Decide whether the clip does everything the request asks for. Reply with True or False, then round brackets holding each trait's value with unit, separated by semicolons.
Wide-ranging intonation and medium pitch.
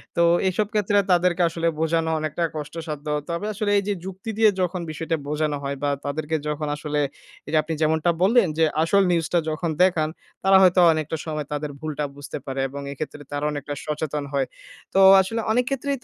False (3.5 semitones; 160 Hz)